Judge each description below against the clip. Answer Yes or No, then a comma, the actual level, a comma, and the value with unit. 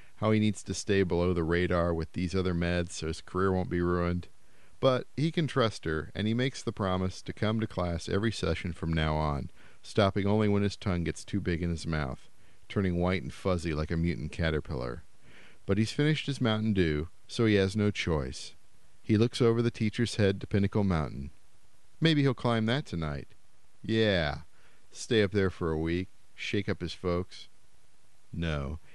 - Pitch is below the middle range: Yes, very low, 95 Hz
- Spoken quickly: No, average, 195 wpm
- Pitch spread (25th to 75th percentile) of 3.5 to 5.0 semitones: Yes, average, 4.5 semitones